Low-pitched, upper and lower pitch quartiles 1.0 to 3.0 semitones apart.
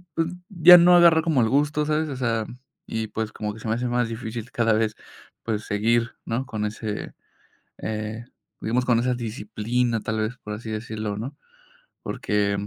Yes: low, 115 Hz; average, 2.7 semitones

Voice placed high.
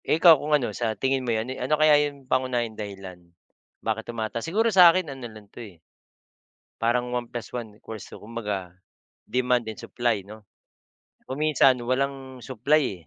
No: low, 125 Hz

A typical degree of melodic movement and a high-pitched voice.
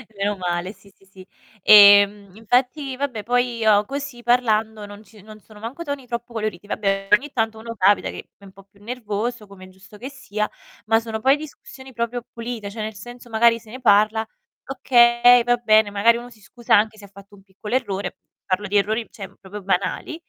Yes: average, 3.1 semitones; high, 220 Hz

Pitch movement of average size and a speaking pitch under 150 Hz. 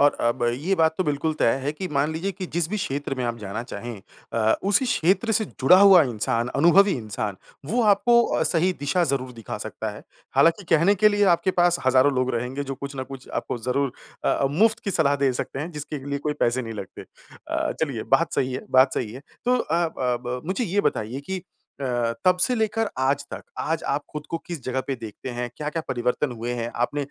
No: wide, 6.1 semitones; medium, 140 Hz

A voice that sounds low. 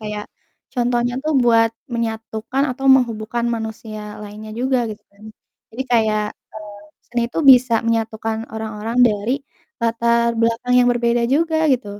No: high, 230 Hz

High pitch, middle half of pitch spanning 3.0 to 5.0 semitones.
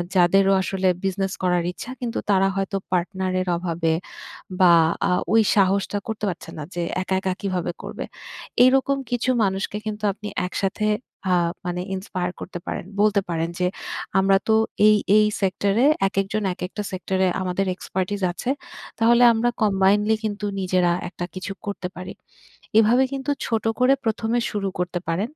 No: high, 195 Hz; narrow, 2.6 semitones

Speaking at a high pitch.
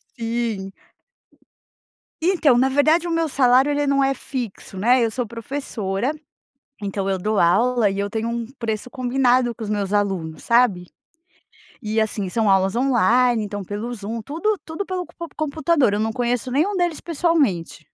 Yes: high, 240 Hz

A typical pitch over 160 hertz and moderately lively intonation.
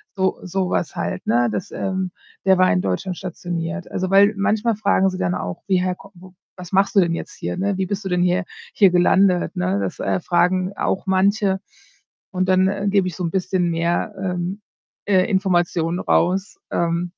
No: medium, 185 Hz; narrow, 1.9 semitones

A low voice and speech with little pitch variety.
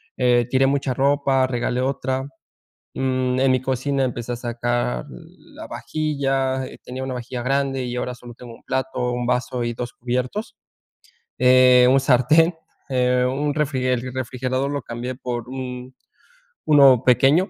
Yes: low, 130 Hz; narrow, 1.4 semitones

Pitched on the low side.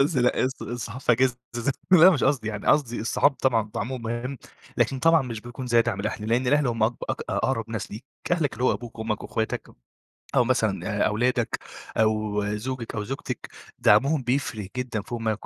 Yes: low, 120 Hz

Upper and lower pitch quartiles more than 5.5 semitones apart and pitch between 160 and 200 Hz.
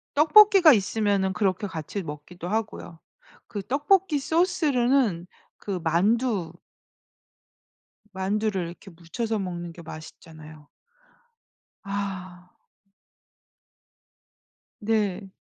No: average, 5.1 semitones; high, 195 Hz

